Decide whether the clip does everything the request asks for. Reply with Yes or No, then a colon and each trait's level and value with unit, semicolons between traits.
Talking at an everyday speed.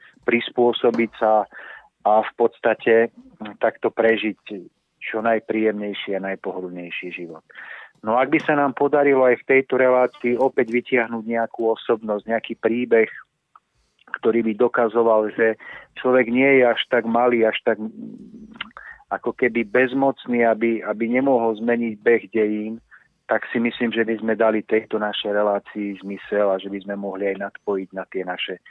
Yes: average, 145 wpm